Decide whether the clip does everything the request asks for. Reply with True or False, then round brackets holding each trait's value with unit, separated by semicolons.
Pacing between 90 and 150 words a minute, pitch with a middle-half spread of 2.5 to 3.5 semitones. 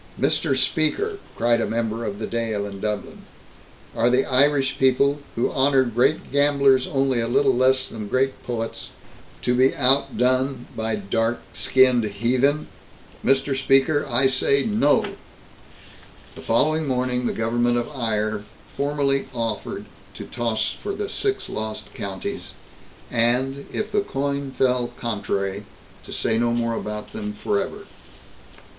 True (140 wpm; 3.2 semitones)